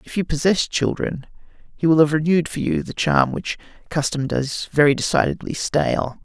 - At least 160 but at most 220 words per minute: Yes, average, 175 wpm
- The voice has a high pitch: No, medium, 140 Hz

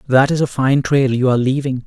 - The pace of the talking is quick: Yes, fast, 260 wpm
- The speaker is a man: Yes, male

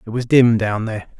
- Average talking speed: No, fast, 250 wpm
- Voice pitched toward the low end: Yes, low, 115 Hz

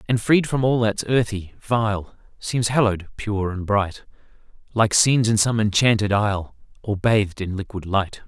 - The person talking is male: Yes, male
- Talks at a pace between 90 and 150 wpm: No, average, 165 wpm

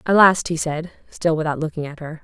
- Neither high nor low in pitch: Yes, medium, 160 Hz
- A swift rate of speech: Yes, fast, 240 wpm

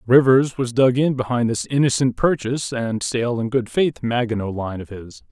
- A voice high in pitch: No, low, 120 Hz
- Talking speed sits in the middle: Yes, average, 190 wpm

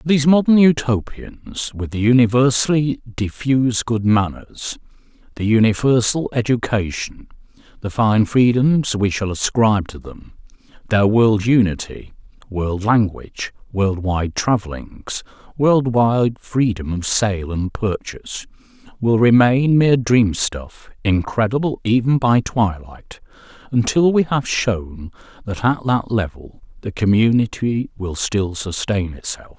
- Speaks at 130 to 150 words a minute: No, slow, 110 wpm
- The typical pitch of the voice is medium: No, low, 110 Hz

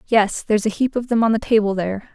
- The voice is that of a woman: Yes, female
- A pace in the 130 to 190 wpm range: No, fast, 280 wpm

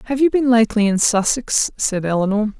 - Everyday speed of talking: Yes, average, 185 wpm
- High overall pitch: Yes, high, 225 Hz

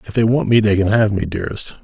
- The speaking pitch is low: Yes, low, 105 Hz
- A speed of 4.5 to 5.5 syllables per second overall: No, 6.8 syllables/s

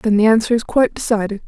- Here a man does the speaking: No, female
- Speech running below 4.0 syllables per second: No, 7.1 syllables/s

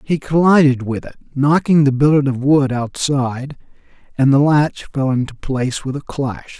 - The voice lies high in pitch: No, medium, 140 Hz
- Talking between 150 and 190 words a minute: Yes, average, 175 wpm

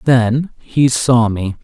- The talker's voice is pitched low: Yes, low, 120 Hz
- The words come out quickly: No, average, 145 wpm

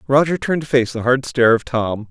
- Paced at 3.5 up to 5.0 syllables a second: No, 6.1 syllables/s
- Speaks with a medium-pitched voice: No, low, 125 Hz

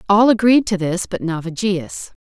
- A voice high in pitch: Yes, high, 195 Hz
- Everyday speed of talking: Yes, average, 160 wpm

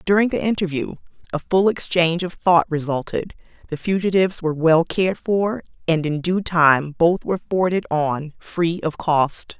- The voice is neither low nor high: Yes, medium, 170 Hz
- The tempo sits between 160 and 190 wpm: Yes, average, 165 wpm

